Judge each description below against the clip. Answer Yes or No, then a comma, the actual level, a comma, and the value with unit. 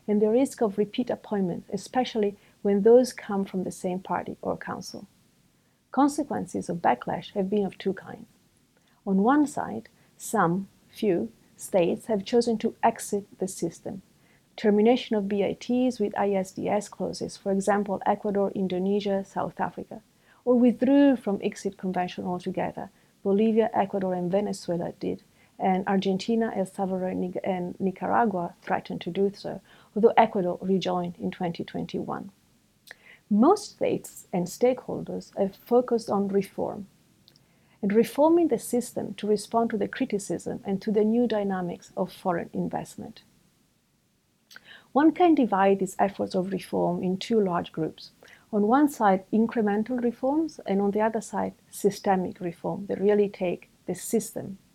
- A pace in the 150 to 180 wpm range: No, average, 140 wpm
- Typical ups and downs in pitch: Yes, average, 3.4 semitones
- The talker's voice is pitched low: No, high, 205 Hz